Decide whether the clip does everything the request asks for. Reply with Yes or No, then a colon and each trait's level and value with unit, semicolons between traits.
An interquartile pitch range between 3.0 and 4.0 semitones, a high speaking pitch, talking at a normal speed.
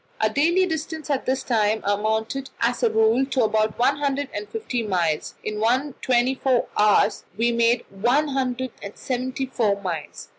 Yes: average, 3.7 semitones; high, 240 Hz; average, 175 wpm